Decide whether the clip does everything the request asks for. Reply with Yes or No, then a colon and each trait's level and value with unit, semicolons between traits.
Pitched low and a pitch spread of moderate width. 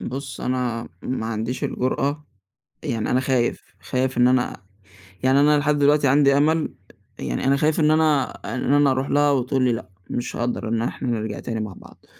Yes: low, 130 Hz; average, 3.1 semitones